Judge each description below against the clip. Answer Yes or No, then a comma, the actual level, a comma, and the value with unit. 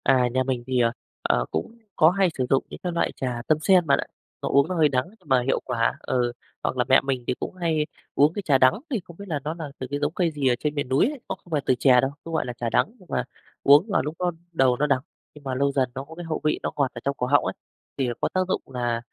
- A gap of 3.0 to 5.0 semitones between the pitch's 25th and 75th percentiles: Yes, average, 4.0 semitones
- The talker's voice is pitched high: No, medium, 140 Hz